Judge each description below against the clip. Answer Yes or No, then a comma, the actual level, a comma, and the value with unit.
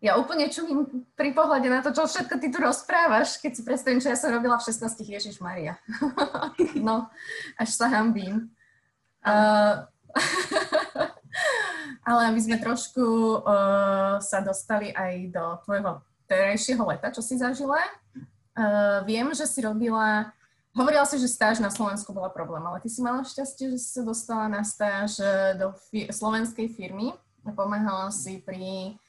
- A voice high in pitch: Yes, high, 225 Hz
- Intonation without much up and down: No, average, 4.9 semitones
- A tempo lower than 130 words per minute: No, average, 155 wpm